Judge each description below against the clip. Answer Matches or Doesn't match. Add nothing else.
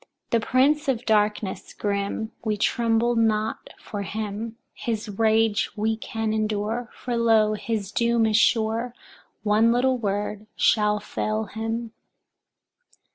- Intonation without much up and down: Matches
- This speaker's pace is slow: Matches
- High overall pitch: Matches